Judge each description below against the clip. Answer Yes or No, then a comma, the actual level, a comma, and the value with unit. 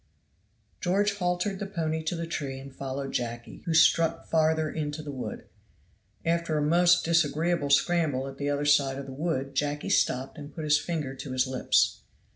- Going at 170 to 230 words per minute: Yes, average, 180 wpm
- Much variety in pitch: No, average, 3.4 semitones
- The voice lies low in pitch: No, medium, 150 Hz